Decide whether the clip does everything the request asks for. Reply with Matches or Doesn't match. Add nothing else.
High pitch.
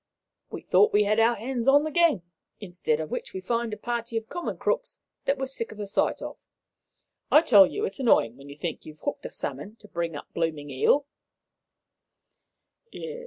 Matches